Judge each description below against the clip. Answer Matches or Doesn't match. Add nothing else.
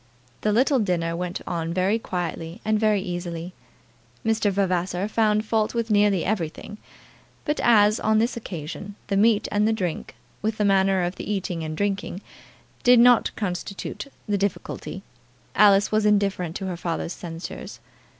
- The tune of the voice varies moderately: Matches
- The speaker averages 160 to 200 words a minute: Doesn't match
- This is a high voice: Matches